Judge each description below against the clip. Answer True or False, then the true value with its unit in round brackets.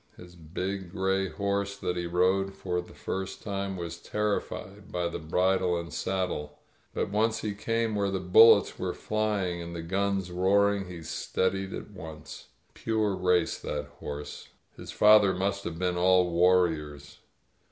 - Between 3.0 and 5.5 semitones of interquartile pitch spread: False (2.4 semitones)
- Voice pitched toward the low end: True (95 Hz)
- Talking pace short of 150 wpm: False (165 wpm)